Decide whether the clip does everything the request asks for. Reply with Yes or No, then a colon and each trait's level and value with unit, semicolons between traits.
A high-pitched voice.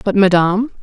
Yes: high, 200 Hz